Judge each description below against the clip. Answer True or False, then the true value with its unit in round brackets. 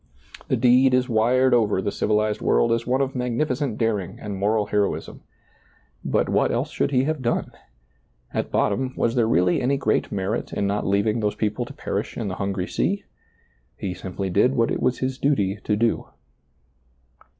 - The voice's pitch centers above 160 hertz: False (115 Hz)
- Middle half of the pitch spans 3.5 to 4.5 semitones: True (3.9 semitones)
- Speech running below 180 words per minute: False (185 wpm)